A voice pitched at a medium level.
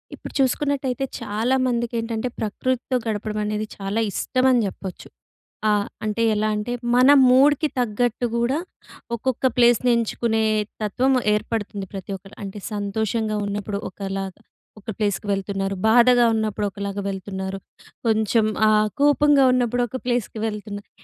No: high, 220 Hz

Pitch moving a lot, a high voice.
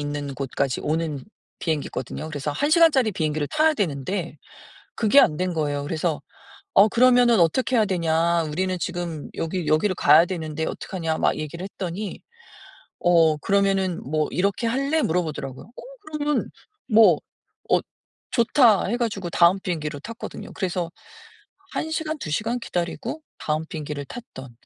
No: wide, 6.1 semitones; medium, 175 Hz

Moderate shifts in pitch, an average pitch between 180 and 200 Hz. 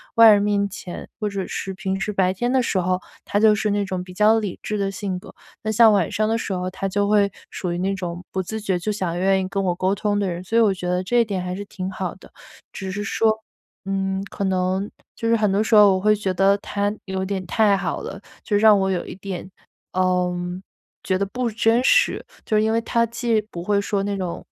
No: narrow, 2.2 semitones; high, 195 Hz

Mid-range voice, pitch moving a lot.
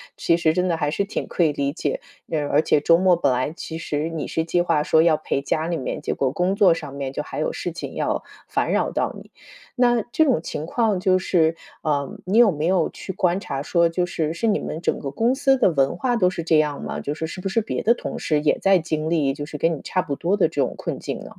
No: medium, 165 Hz; average, 3.8 semitones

